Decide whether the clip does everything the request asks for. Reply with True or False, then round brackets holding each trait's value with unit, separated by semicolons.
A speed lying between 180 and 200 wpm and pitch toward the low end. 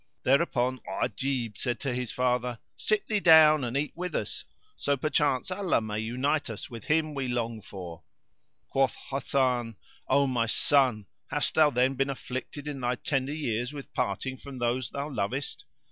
False (165 wpm; 130 Hz)